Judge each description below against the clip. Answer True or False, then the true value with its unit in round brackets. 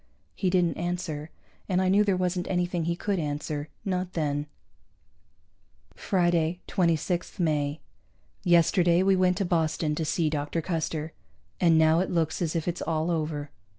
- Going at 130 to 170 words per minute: True (150 wpm)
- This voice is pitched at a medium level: True (170 Hz)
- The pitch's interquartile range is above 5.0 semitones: False (2.4 semitones)